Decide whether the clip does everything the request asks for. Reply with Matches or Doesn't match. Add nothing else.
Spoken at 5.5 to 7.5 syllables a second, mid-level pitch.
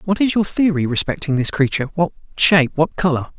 Matches